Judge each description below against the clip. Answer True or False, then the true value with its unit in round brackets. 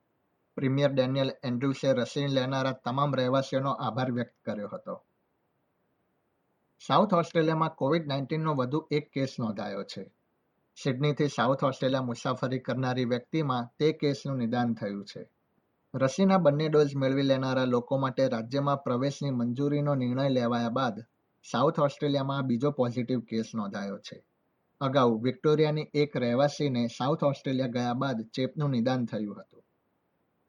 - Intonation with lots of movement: False (2.6 semitones)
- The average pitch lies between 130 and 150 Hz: True (135 Hz)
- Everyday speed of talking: True (125 wpm)